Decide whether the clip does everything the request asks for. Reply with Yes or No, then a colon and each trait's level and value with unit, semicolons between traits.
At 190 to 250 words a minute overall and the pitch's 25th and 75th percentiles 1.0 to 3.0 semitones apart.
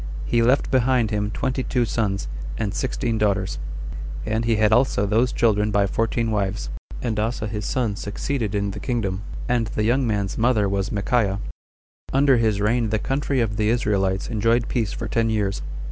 No: average, 175 wpm; narrow, 2.6 semitones